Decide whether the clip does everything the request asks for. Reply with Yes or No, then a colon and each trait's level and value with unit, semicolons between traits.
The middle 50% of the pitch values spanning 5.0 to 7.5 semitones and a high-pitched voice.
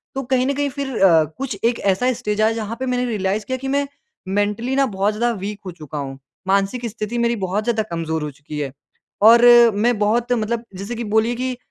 No: average, 3.9 semitones; high, 220 Hz